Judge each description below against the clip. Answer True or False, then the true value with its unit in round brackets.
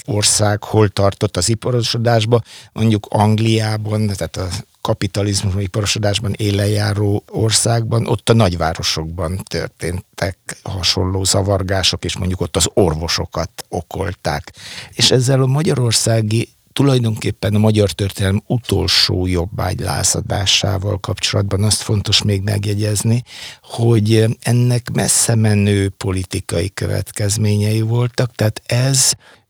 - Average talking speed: False (100 wpm)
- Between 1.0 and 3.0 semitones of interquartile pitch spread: True (2.6 semitones)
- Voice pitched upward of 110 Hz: False (105 Hz)